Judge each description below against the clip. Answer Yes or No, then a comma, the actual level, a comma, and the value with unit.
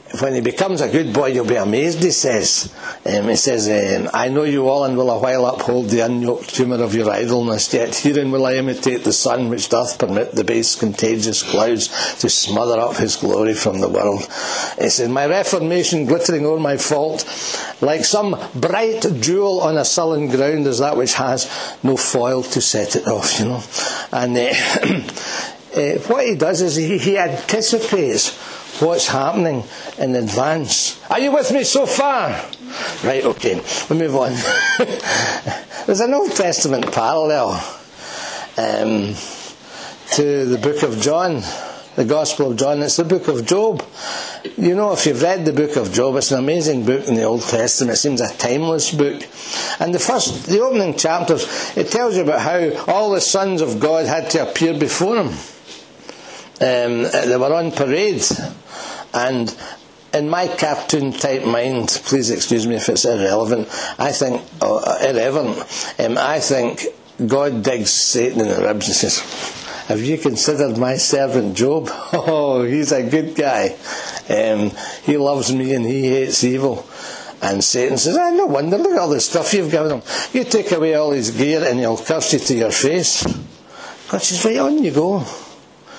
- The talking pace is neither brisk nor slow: Yes, average, 175 wpm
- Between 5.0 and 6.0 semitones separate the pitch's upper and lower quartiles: Yes, wide, 5.4 semitones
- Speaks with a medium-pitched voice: Yes, medium, 145 Hz